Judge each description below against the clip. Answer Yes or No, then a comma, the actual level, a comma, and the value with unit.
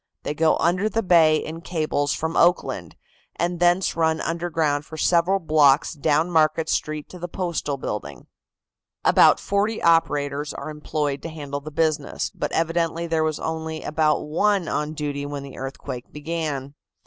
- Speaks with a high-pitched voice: No, medium, 155 Hz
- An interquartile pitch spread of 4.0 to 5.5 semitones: No, narrow, 2.4 semitones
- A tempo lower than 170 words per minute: Yes, average, 160 wpm